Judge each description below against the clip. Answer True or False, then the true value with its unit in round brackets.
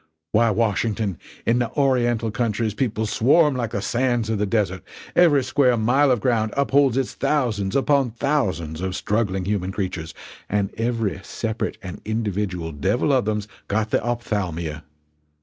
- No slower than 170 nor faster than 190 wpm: False (150 wpm)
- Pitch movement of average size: True (3.7 semitones)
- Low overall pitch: True (110 Hz)